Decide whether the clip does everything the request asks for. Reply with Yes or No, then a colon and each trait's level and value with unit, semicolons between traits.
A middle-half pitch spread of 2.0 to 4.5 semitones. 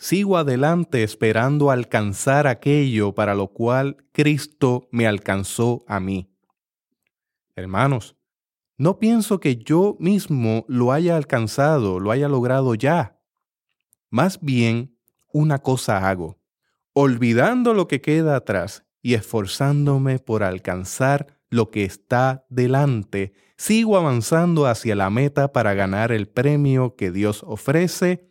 No: average, 5.2 semitones